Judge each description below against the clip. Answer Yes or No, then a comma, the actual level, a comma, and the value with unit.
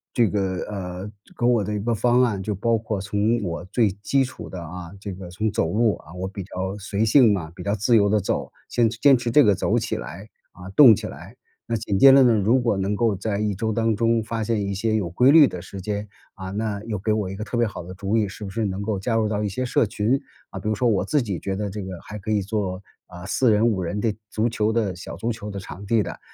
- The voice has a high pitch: No, low, 105 Hz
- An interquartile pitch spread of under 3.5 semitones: Yes, average, 2.8 semitones